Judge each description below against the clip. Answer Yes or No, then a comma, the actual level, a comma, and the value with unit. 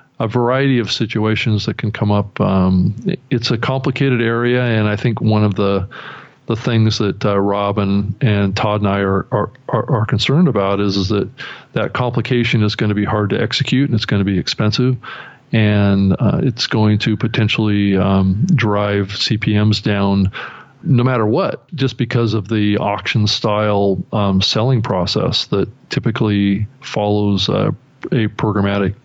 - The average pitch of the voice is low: Yes, low, 105 Hz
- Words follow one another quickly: No, average, 165 wpm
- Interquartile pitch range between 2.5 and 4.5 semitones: Yes, average, 2.9 semitones